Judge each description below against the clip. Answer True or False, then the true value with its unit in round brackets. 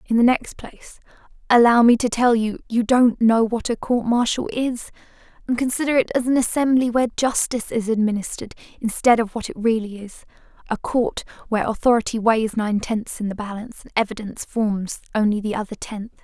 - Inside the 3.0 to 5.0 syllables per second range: False (5.7 syllables/s)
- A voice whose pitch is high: True (230 Hz)